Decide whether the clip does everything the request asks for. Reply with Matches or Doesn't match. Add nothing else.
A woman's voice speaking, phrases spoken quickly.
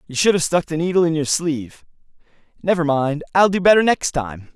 Doesn't match